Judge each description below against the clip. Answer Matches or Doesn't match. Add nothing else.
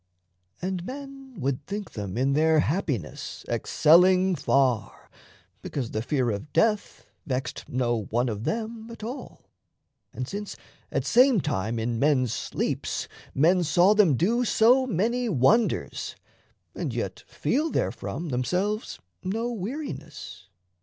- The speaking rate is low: Matches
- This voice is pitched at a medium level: Matches